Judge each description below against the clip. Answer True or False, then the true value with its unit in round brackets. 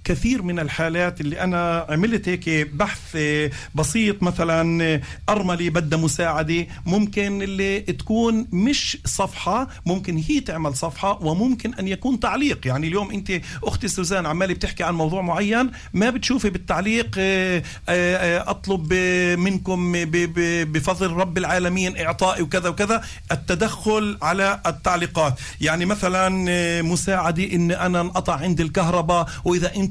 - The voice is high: False (180 Hz)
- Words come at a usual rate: True (120 wpm)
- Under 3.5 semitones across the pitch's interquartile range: True (2.7 semitones)